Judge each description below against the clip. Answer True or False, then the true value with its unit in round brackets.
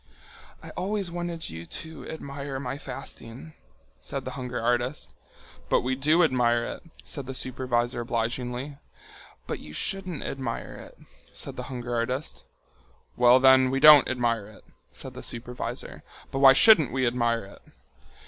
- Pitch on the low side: True (130 Hz)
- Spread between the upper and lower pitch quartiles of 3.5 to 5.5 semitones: False (3.1 semitones)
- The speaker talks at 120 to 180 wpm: True (150 wpm)